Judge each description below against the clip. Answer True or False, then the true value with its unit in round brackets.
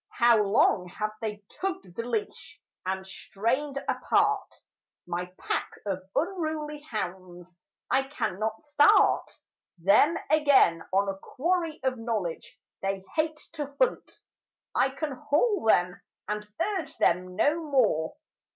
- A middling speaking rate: False (125 wpm)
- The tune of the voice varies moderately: False (7.7 semitones)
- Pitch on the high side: True (230 Hz)